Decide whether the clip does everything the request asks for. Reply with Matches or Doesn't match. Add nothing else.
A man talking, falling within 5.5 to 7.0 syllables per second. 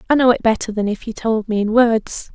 Doesn't match